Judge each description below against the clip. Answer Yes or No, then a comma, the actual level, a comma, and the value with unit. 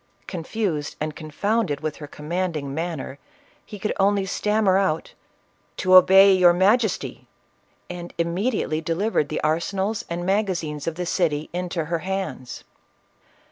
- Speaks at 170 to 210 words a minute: No, average, 145 wpm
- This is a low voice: No, medium, 175 Hz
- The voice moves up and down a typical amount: Yes, average, 3.8 semitones